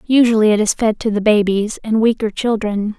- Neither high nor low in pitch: No, high, 215 Hz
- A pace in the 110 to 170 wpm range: No, average, 200 wpm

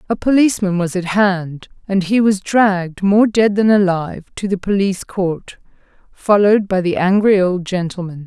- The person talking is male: No, female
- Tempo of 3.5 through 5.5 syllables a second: Yes, 4.9 syllables/s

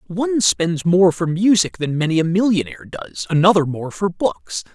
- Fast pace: No, average, 175 wpm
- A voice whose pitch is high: No, medium, 175 Hz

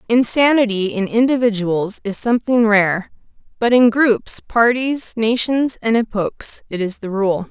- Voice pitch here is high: Yes, high, 225 Hz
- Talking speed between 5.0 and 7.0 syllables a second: No, 4.2 syllables/s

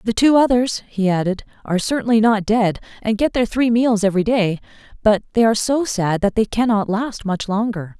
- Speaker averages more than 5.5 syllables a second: No, 5.4 syllables/s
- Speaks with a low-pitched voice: No, high, 215 Hz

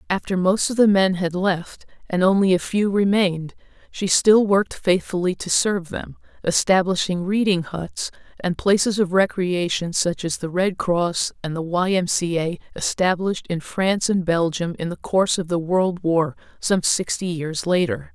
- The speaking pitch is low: No, medium, 180 Hz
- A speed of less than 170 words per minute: No, average, 175 wpm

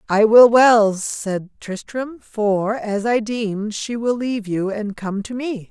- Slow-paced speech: No, average, 180 wpm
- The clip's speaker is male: No, female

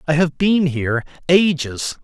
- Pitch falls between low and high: Yes, medium, 155 Hz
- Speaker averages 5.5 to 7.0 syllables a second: No, 4.4 syllables/s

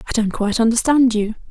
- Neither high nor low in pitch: No, high, 230 Hz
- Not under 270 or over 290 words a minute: No, average, 200 wpm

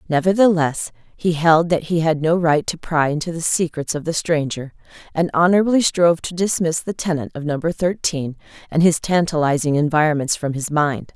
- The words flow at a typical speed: Yes, average, 180 wpm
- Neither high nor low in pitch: Yes, medium, 160 Hz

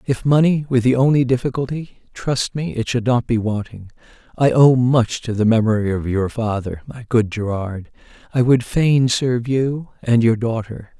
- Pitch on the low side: Yes, low, 120 Hz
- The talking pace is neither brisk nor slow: Yes, average, 175 wpm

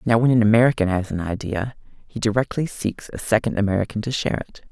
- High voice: No, low, 110 Hz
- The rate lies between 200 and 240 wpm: Yes, fast, 205 wpm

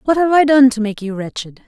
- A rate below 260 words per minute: No, fast, 285 wpm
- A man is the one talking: No, female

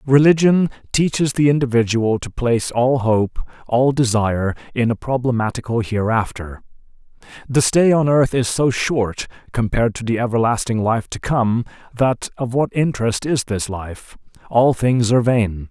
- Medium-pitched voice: No, low, 120 Hz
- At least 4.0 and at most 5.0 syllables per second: Yes, 4.7 syllables/s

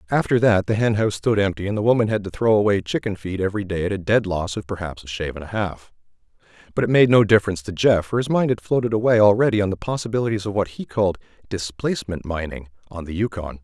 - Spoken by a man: Yes, male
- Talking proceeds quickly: Yes, fast, 240 wpm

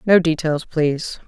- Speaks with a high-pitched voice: No, medium, 160 Hz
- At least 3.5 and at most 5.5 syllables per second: Yes, 4.6 syllables/s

